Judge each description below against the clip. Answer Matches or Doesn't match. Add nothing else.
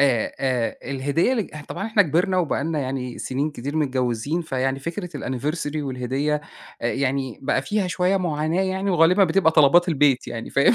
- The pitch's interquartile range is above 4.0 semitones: Matches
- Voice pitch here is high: Doesn't match